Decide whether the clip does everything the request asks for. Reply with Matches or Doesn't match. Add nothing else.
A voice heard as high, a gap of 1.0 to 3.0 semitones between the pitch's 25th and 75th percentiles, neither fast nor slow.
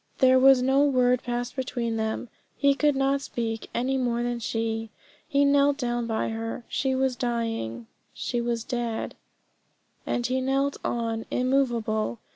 Matches